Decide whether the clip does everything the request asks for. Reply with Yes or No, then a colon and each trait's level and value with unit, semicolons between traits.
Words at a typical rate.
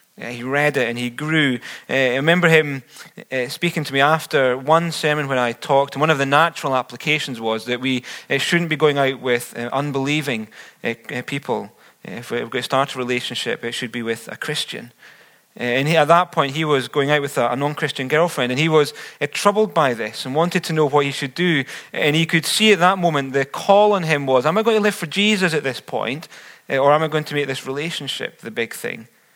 No: fast, 220 wpm